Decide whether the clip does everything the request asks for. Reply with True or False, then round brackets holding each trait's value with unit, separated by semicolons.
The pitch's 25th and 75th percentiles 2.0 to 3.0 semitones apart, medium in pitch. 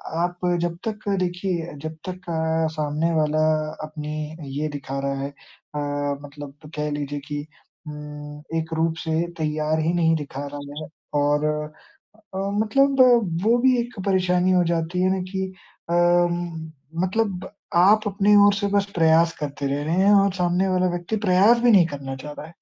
False (3.7 semitones; 165 Hz)